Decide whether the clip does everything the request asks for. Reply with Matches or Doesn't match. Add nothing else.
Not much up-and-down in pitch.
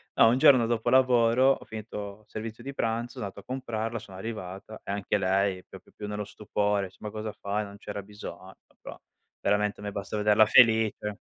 Matches